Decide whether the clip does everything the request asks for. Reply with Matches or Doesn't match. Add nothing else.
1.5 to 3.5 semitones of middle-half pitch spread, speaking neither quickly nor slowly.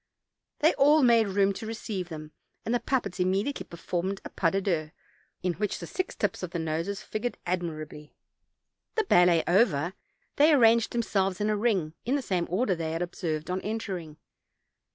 Doesn't match